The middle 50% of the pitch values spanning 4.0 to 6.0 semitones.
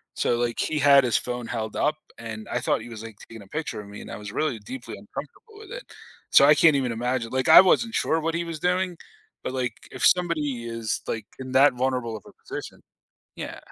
Yes: average, 5.1 semitones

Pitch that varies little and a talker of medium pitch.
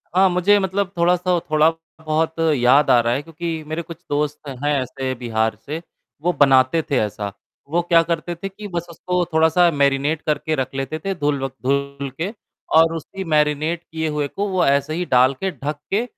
No: average, 3.6 semitones; medium, 155 Hz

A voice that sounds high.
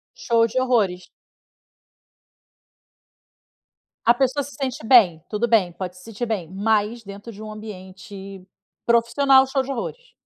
Yes: high, 220 Hz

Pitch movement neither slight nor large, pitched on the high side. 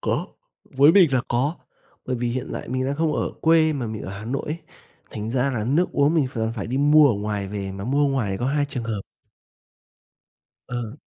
No: average, 4.6 semitones; low, 130 Hz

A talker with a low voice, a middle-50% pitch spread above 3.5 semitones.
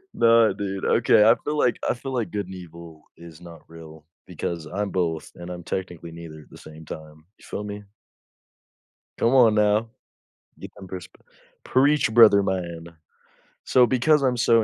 Yes: very low, 95 Hz; wide, 5.5 semitones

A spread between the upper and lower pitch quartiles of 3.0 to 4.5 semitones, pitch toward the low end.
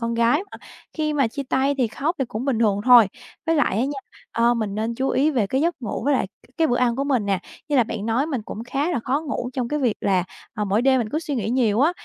No: average, 3.9 semitones; very high, 250 Hz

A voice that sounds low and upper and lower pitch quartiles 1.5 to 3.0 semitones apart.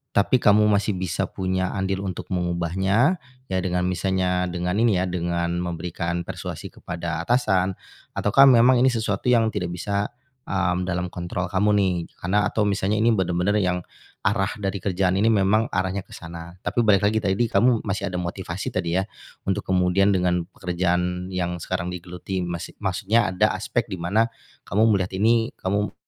Yes: very low, 95 Hz; narrow, 2.5 semitones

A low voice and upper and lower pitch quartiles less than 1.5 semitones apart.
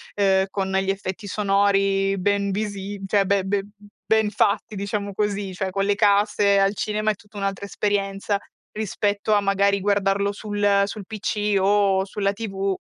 No: high, 200 Hz; narrow, 0.9 semitones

